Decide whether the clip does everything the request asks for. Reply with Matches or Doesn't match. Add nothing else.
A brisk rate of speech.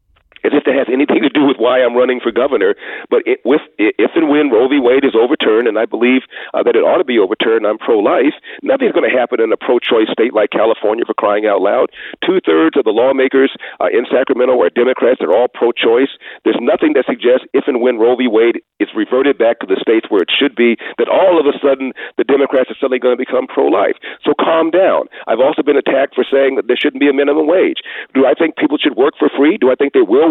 Matches